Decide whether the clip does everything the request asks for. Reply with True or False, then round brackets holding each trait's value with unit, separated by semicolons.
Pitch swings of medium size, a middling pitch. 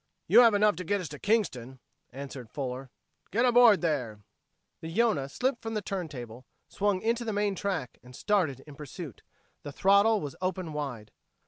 False (7.5 semitones; 175 Hz)